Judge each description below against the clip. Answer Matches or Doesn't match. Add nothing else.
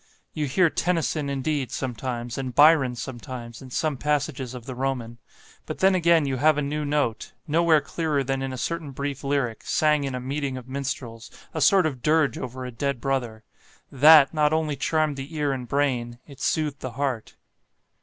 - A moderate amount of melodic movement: Matches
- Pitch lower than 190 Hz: Matches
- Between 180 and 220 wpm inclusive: Matches